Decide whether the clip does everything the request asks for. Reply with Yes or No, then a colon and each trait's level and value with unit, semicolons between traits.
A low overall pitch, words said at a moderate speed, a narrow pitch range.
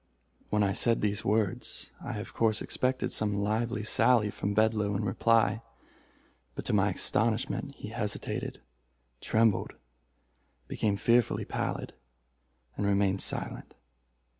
No: low, 105 Hz; slow, 120 wpm; narrow, 2.0 semitones